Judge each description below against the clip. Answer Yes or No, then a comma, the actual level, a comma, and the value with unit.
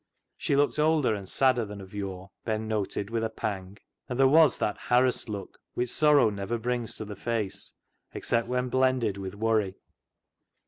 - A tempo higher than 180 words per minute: No, average, 175 wpm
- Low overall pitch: Yes, low, 110 Hz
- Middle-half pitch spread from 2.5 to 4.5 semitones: Yes, average, 3.7 semitones